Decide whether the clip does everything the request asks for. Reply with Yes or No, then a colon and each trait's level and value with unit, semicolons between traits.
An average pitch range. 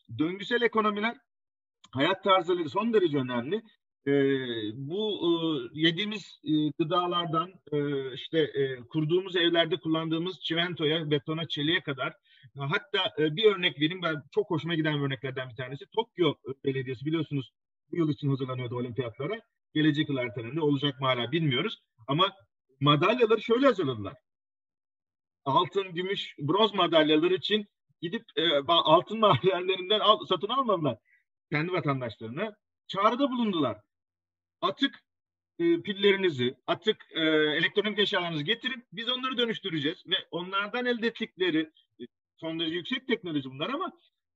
No: wide, 6.4 semitones